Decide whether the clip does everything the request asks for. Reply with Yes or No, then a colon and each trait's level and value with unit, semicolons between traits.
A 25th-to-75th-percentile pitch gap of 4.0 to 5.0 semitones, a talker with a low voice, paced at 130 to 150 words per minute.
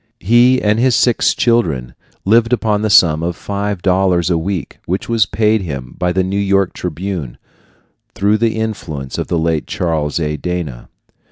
No: average, 4.7 semitones; very low, 95 Hz; average, 170 wpm